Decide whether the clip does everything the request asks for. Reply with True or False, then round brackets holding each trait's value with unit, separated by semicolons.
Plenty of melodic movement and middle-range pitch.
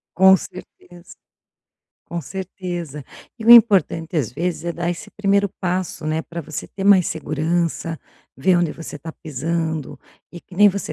False (2.8 semitones; 175 Hz)